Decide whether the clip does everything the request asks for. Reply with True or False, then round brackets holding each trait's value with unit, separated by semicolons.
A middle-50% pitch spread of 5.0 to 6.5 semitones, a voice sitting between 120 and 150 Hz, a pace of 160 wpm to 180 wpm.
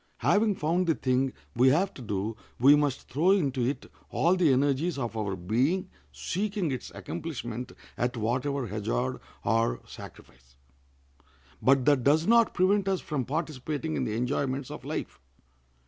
False (5.5 semitones; 135 Hz; 150 wpm)